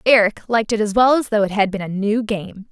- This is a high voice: Yes, high, 215 Hz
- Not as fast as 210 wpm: No, fast, 290 wpm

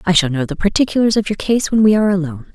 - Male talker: No, female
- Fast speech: Yes, fast, 285 wpm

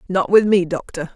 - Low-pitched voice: No, medium, 180 Hz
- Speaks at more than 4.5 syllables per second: Yes, 5.2 syllables/s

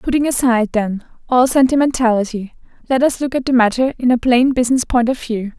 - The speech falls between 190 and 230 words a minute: Yes, average, 195 wpm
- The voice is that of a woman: Yes, female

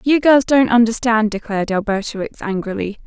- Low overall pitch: No, high, 225 Hz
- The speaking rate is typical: Yes, average, 155 wpm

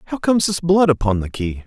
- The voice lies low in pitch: No, medium, 150 Hz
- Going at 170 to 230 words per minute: No, fast, 250 wpm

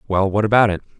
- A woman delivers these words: No, male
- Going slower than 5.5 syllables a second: No, 7.4 syllables/s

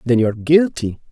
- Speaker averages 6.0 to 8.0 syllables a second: Yes, 6.5 syllables/s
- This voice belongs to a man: Yes, male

